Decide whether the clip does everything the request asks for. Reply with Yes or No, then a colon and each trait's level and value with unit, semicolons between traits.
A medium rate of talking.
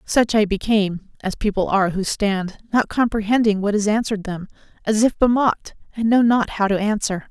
Yes: average, 190 wpm